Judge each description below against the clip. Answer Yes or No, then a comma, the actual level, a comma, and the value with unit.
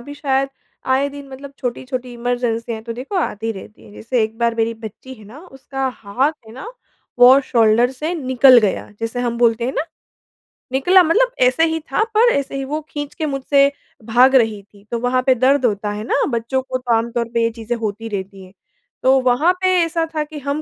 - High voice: Yes, very high, 255 Hz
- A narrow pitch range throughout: No, average, 3.5 semitones